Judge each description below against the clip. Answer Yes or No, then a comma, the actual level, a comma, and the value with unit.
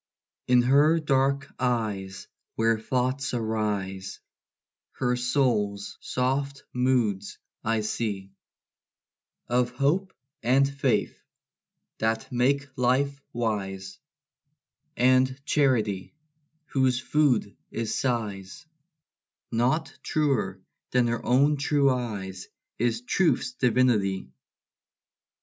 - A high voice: No, low, 125 Hz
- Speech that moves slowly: Yes, slow, 85 wpm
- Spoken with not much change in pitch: No, average, 4.1 semitones